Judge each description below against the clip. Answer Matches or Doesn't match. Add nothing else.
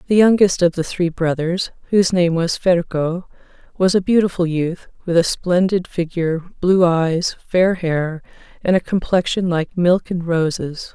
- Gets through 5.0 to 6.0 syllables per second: Doesn't match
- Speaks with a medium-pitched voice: Matches